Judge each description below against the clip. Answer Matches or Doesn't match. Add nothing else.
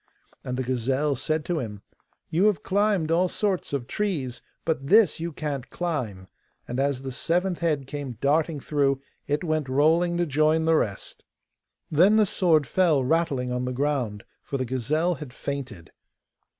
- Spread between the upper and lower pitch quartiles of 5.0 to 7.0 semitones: Doesn't match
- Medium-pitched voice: Matches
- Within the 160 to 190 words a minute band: Matches